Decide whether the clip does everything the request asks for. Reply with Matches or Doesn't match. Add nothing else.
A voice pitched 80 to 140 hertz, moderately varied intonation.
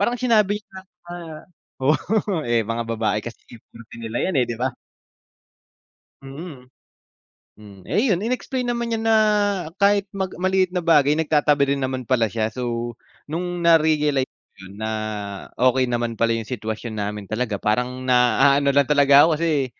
Doesn't match